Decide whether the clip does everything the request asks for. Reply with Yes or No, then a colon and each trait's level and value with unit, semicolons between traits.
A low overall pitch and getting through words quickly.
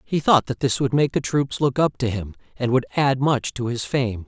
Yes: low, 130 Hz; fast, 265 wpm